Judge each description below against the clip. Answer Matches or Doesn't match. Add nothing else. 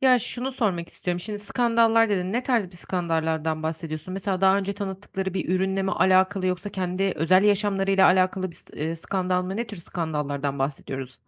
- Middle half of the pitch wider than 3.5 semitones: Doesn't match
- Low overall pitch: Doesn't match